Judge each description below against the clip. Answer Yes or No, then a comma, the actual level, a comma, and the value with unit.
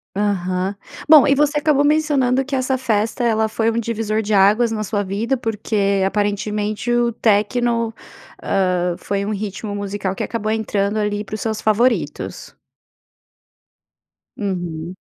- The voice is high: Yes, high, 215 Hz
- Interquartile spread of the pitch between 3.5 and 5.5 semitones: No, average, 2.9 semitones